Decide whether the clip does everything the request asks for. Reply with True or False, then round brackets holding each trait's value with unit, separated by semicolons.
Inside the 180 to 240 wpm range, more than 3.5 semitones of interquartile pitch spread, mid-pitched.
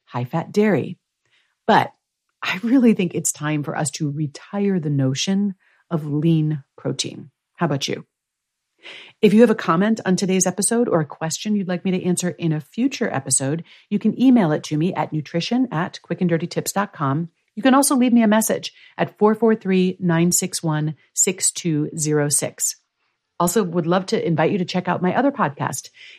False (170 wpm; 4.9 semitones; 180 Hz)